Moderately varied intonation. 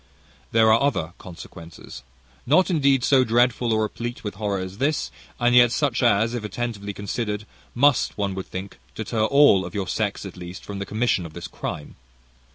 Yes: average, 3.7 semitones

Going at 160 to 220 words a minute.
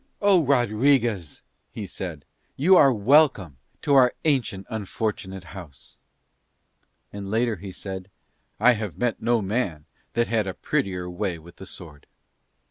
No: slow, 135 wpm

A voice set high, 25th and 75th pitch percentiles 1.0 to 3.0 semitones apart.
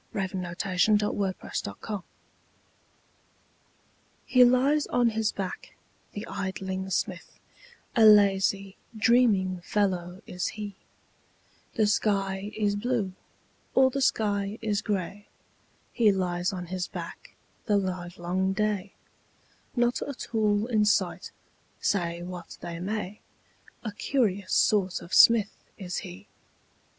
Yes: high, 200 Hz; narrow, 2.6 semitones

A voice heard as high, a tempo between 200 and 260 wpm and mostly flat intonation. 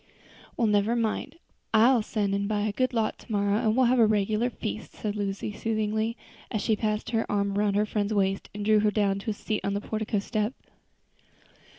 Yes: high, 215 Hz; fast, 205 wpm; narrow, 1.5 semitones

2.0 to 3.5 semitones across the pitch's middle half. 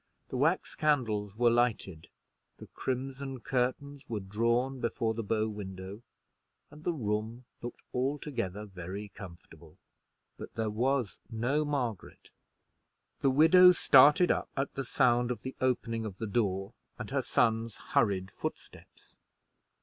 No: average, 4.3 semitones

